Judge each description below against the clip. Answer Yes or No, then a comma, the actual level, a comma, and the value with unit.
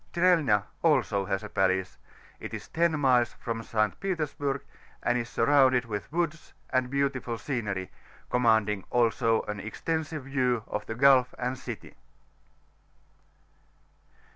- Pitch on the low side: Yes, low, 125 Hz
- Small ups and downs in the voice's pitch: No, average, 4.2 semitones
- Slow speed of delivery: Yes, slow, 125 wpm